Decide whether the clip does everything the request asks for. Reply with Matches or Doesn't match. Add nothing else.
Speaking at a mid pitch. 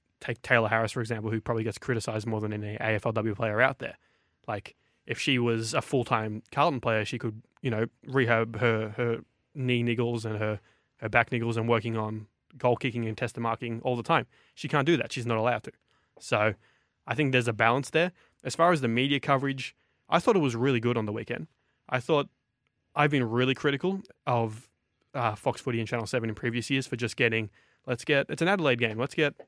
Doesn't match